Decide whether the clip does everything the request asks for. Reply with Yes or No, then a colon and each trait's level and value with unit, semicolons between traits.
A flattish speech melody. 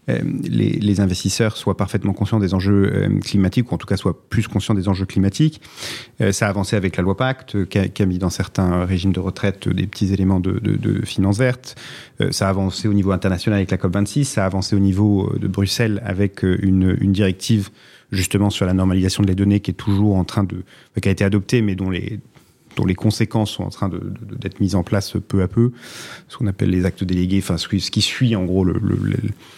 Yes: narrow, 2.2 semitones